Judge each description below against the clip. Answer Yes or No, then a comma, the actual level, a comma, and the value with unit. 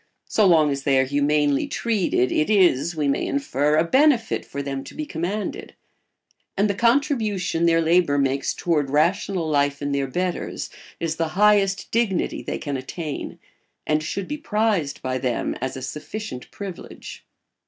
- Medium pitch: Yes, medium, 165 Hz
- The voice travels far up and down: Yes, wide, 6.1 semitones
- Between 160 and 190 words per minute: Yes, average, 165 wpm